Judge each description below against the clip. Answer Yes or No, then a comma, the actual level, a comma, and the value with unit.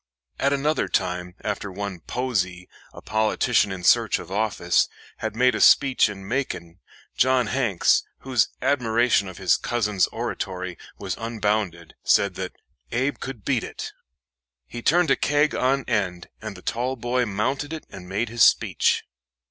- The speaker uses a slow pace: No, average, 155 wpm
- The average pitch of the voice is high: No, low, 110 Hz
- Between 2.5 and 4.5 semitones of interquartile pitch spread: No, average, 5.2 semitones